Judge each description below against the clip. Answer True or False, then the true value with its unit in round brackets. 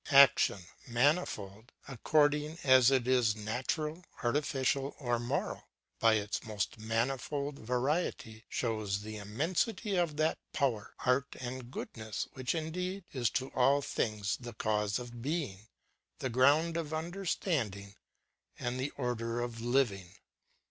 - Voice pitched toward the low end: True (125 Hz)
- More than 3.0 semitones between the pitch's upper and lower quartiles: True (4.7 semitones)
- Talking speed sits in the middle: False (130 wpm)